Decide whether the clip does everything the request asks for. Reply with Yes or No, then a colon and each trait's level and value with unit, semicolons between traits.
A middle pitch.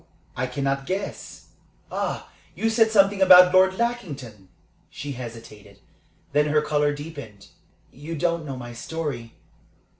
Yes: medium, 145 Hz